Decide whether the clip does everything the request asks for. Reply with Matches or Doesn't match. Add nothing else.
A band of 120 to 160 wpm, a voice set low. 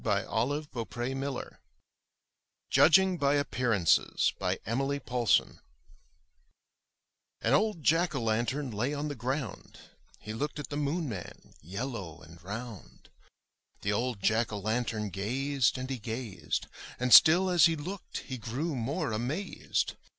Matches